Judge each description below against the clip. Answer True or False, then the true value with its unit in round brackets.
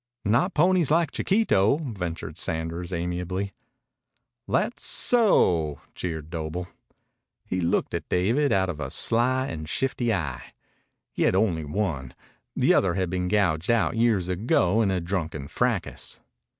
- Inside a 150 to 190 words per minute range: False (135 wpm)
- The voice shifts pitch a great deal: True (5.7 semitones)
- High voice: False (95 Hz)